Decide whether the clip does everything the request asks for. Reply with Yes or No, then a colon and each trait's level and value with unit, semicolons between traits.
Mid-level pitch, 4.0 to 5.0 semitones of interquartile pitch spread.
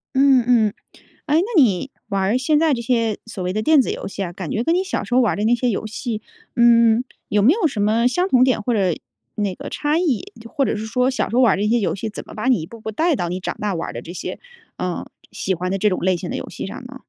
No: high, 230 Hz; average, 4.5 semitones